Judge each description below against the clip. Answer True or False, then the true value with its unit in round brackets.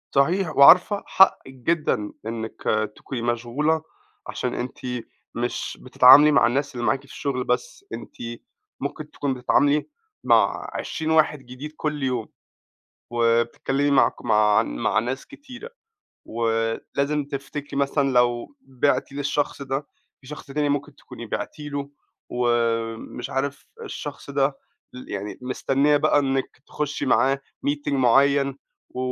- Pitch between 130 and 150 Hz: True (135 Hz)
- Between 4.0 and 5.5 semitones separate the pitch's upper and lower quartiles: False (3.1 semitones)